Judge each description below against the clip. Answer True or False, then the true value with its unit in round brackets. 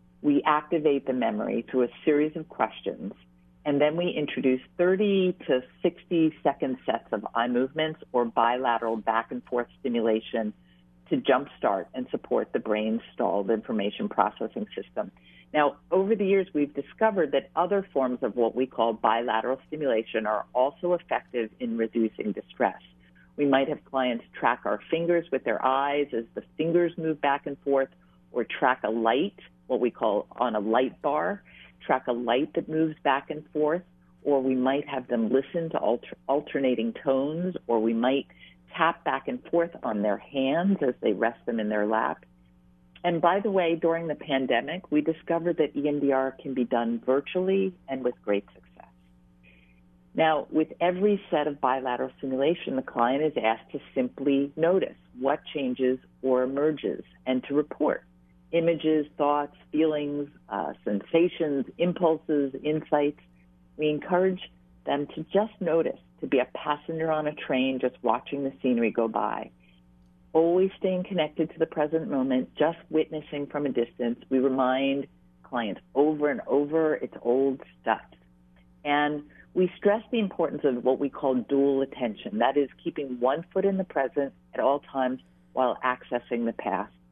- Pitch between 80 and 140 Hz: True (135 Hz)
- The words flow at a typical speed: True (160 wpm)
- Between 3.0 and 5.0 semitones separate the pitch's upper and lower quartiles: False (5.4 semitones)